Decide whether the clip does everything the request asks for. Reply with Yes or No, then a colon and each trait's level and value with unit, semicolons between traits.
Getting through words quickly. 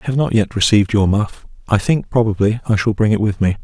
Yes: fast, 265 wpm